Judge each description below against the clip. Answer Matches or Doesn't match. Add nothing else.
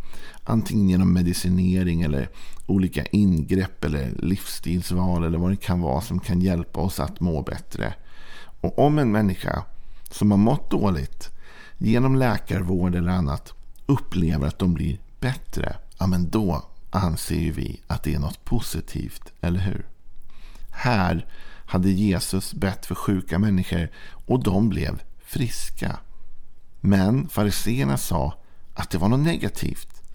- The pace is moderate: Matches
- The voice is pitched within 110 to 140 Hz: Doesn't match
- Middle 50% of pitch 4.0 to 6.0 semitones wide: Doesn't match